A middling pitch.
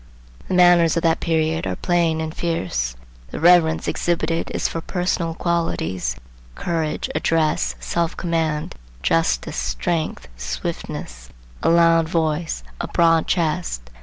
Yes: medium, 160 Hz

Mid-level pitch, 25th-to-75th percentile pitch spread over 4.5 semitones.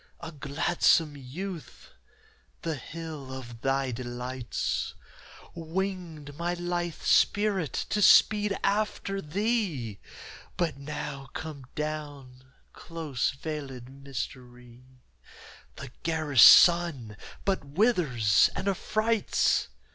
Yes: medium, 150 Hz; average, 4.9 semitones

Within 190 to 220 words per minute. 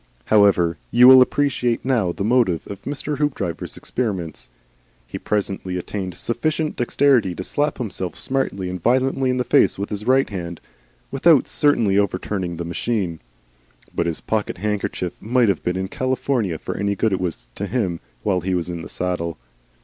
No: average, 170 wpm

